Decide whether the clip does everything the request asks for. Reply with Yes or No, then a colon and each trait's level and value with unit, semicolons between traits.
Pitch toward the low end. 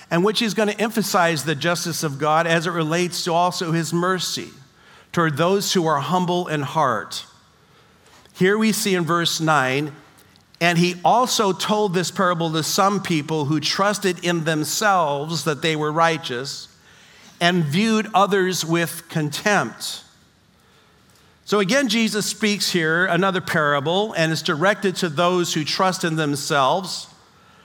No: medium, 170 Hz